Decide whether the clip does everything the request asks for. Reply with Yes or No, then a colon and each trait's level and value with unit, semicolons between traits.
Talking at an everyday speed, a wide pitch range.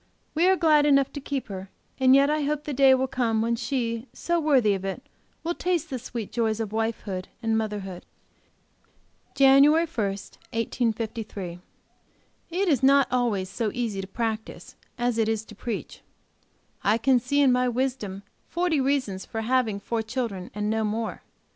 No: average, 170 wpm; average, 4.1 semitones